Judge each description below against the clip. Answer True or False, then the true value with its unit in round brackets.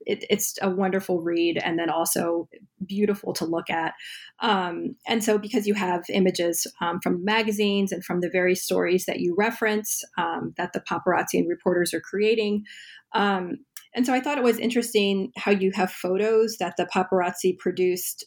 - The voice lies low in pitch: False (195 Hz)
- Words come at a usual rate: True (175 wpm)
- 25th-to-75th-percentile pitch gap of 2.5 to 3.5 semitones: True (3.2 semitones)